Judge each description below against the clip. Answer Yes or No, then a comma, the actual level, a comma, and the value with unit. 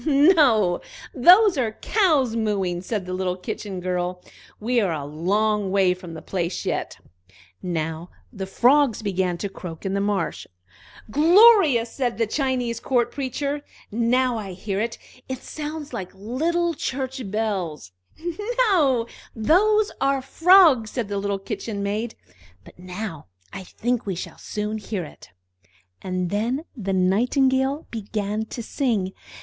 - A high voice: Yes, high, 220 Hz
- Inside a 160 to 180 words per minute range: No, average, 145 wpm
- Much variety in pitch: Yes, wide, 5.9 semitones